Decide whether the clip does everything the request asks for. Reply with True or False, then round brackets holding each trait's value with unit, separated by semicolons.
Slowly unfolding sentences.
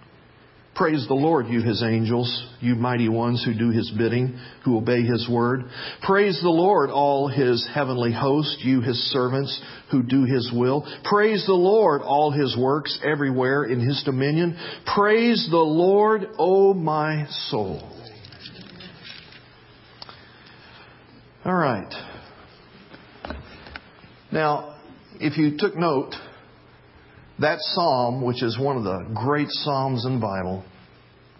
True (130 wpm)